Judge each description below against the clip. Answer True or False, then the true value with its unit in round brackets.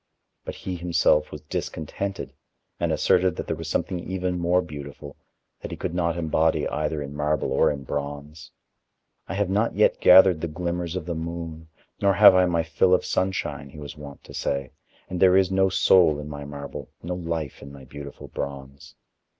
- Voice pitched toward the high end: False (80 Hz)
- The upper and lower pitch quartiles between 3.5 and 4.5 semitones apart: True (3.8 semitones)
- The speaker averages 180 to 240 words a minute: True (190 wpm)